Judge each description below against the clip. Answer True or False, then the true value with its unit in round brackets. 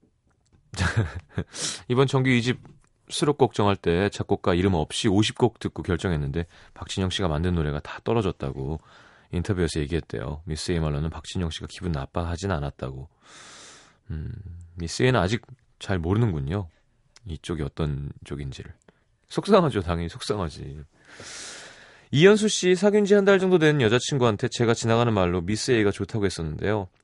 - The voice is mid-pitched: False (100 Hz)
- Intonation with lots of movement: True (6.4 semitones)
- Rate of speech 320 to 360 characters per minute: True (325 characters per minute)